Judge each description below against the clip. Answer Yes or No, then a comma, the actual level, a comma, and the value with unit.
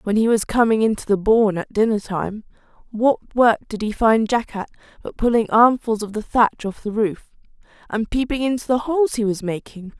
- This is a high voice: Yes, high, 225 Hz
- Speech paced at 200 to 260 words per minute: Yes, fast, 205 wpm